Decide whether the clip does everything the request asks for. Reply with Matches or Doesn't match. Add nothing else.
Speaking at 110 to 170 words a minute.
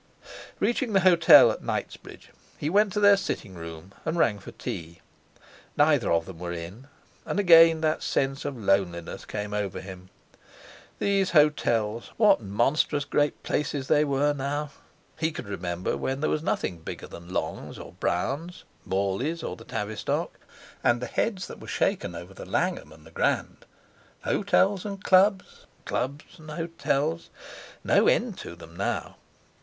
Matches